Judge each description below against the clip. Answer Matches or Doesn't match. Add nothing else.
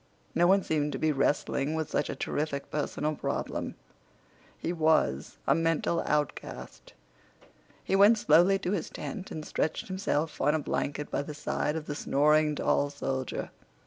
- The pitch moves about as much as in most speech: Doesn't match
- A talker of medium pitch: Matches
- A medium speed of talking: Matches